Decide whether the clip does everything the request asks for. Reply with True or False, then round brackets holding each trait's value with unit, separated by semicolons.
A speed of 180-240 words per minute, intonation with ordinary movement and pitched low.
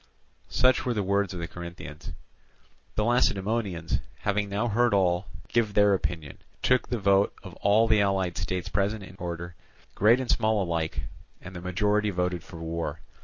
False (170 wpm; 3.3 semitones; 100 Hz)